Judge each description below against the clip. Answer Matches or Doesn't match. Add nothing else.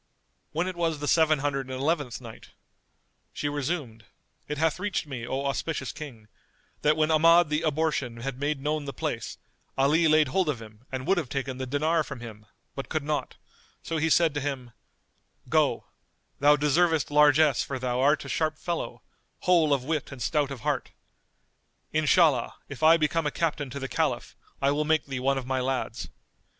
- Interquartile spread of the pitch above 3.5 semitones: Doesn't match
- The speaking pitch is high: Doesn't match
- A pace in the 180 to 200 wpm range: Matches